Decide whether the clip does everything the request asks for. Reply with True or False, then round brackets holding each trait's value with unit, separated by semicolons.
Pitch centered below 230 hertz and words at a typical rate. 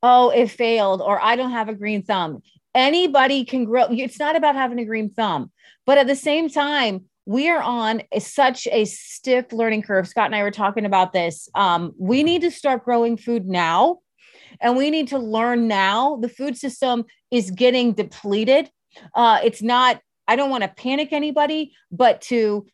False (240 Hz; 190 wpm)